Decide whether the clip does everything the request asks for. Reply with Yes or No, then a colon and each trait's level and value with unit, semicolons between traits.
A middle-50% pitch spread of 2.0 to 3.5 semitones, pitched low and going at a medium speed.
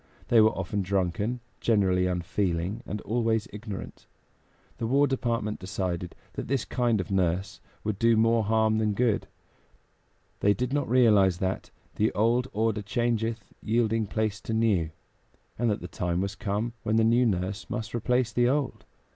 Yes: average, 3.1 semitones; low, 110 Hz; average, 160 wpm